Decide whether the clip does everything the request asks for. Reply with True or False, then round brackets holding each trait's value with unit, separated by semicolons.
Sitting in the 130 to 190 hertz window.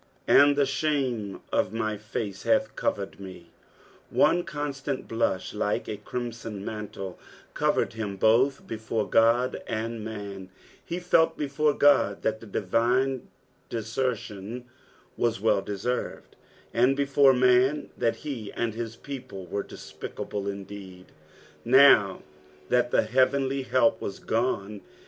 False (115 Hz)